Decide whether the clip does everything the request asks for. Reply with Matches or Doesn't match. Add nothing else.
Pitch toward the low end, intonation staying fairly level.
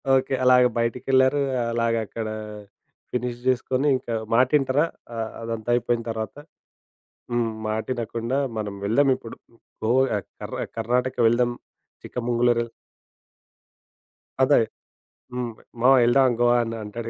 Matches